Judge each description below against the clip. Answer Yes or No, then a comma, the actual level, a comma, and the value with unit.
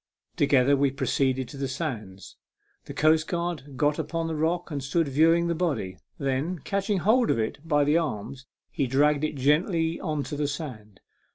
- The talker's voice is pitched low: No, medium, 145 Hz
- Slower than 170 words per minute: No, average, 180 wpm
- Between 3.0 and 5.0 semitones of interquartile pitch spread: Yes, average, 3.6 semitones